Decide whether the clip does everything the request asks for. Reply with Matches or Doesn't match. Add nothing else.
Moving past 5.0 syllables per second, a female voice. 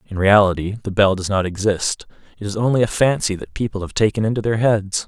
Doesn't match